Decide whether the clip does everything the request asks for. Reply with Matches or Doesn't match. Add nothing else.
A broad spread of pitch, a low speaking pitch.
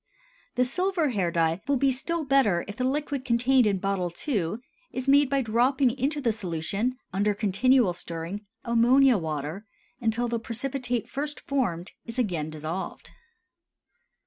Doesn't match